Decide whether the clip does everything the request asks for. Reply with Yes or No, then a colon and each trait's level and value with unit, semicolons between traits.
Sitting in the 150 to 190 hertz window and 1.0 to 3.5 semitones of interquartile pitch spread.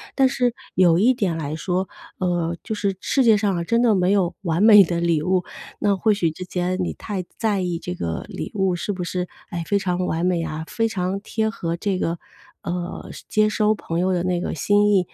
Yes: medium, 185 Hz; average, 3.2 semitones